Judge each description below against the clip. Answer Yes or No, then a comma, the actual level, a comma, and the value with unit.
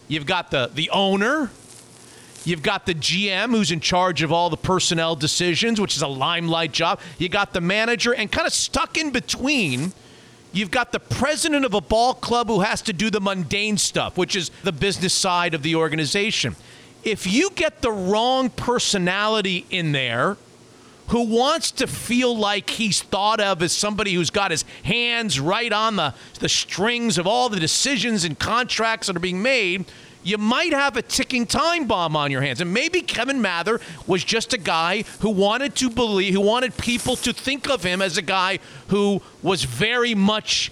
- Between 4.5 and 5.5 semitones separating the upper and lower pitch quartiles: Yes, average, 5.2 semitones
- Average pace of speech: Yes, average, 190 wpm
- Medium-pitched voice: No, high, 200 Hz